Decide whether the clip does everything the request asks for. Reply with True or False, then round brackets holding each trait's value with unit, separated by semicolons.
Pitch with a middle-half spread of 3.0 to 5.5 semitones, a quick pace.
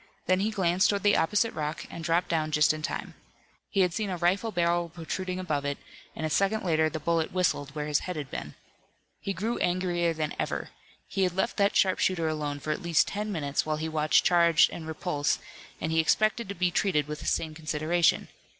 True (3.3 semitones; 215 wpm)